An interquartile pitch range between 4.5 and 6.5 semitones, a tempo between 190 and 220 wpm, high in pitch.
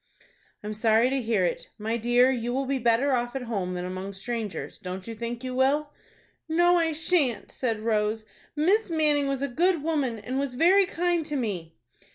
Yes: average, 5.1 semitones; average, 195 wpm; very high, 250 Hz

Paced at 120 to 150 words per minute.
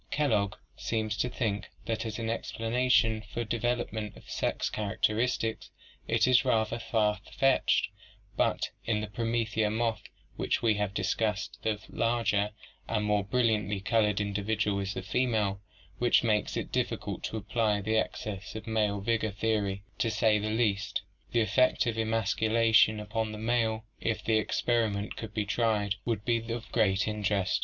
No: average, 160 wpm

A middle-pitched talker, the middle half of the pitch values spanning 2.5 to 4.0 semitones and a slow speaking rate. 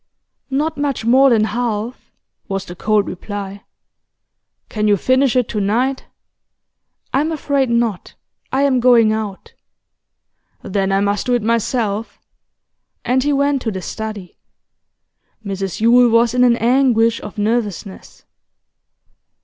No: high, 230 Hz; average, 3.6 semitones; slow, 130 wpm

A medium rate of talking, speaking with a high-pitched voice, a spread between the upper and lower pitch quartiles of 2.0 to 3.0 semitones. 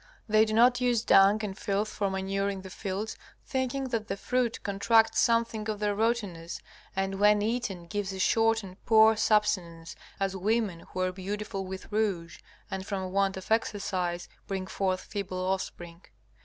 Yes: average, 165 wpm; high, 200 Hz; narrow, 2.5 semitones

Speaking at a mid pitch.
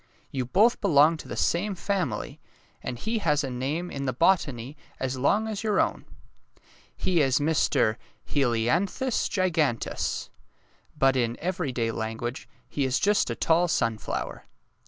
Yes: medium, 145 Hz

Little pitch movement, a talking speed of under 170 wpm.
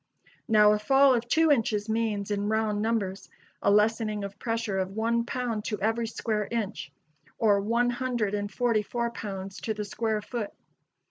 No: narrow, 2.2 semitones; average, 175 wpm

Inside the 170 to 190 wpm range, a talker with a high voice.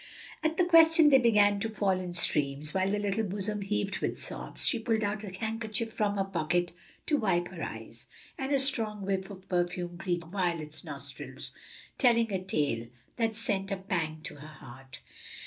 Yes: average, 180 wpm; high, 195 Hz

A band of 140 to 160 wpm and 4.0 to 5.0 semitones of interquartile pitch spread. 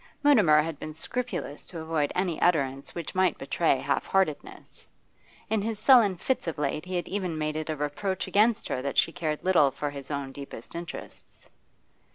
No: average, 185 wpm; average, 4.4 semitones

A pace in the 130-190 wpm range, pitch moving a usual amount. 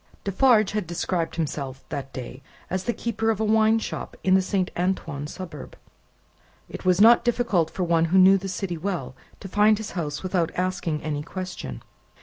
Yes: average, 180 wpm; average, 4.1 semitones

